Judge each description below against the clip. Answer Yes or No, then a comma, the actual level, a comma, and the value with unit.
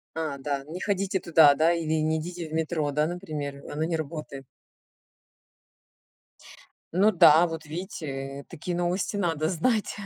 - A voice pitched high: No, medium, 160 Hz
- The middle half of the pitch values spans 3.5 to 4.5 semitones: No, average, 2.8 semitones